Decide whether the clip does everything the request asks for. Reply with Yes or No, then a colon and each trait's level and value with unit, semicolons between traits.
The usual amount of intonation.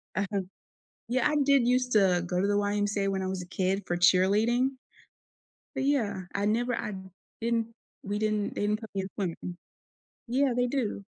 Yes: average, 3.9 semitones